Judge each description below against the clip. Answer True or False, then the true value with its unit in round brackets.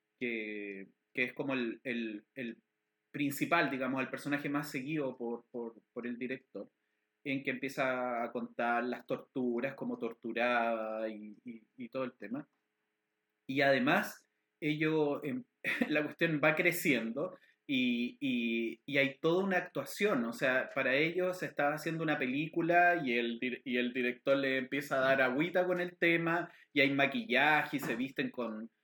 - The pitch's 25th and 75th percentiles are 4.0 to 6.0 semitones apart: True (4.7 semitones)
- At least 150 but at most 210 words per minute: True (160 wpm)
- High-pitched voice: False (135 Hz)